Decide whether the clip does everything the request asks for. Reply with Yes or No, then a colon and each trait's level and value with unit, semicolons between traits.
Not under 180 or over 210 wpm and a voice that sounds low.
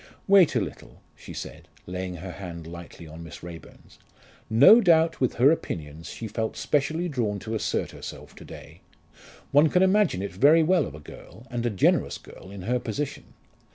Yes: average, 185 wpm; low, 110 Hz